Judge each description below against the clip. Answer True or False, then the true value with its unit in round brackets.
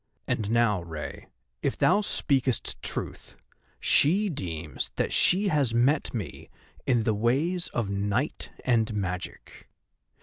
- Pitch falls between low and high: False (120 Hz)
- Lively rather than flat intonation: True (6.1 semitones)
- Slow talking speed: True (125 wpm)